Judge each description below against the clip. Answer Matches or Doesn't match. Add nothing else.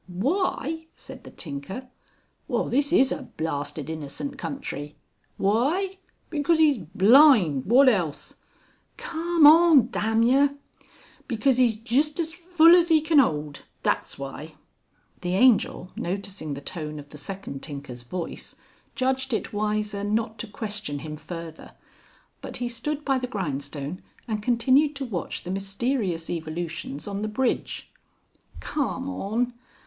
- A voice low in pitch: Doesn't match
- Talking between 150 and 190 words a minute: Doesn't match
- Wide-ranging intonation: Matches